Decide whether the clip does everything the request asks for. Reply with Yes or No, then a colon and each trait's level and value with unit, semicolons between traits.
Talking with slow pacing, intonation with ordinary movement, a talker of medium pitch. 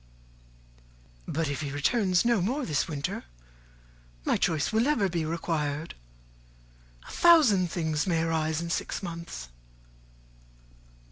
Yes: slow, 120 wpm; average, 4.1 semitones; medium, 165 Hz